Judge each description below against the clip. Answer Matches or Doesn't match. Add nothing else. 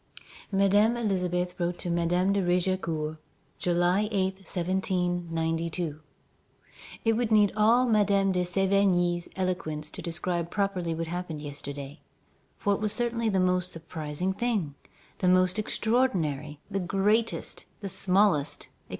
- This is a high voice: Doesn't match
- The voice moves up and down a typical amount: Matches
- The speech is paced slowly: Matches